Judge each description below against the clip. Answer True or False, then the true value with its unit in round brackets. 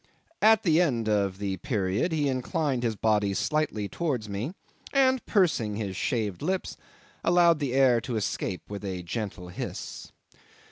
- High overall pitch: False (120 Hz)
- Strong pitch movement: True (7.4 semitones)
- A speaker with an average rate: True (150 wpm)